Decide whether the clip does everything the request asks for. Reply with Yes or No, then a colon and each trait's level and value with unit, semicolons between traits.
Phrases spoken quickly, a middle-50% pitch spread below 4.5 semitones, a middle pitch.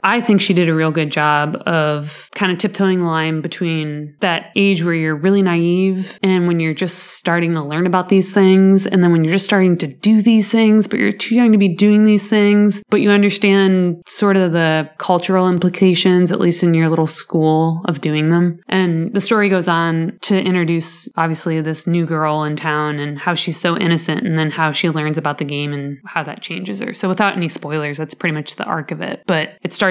Yes: fast, 225 wpm; average, 3.5 semitones; medium, 175 Hz